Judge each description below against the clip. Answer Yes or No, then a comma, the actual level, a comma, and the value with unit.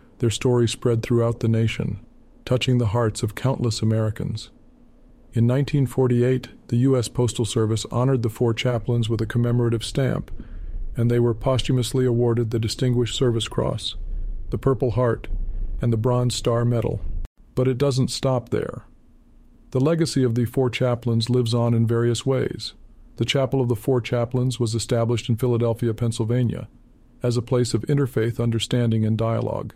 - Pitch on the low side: Yes, low, 120 Hz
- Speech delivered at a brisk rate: No, average, 155 wpm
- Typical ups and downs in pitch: No, narrow, 1.7 semitones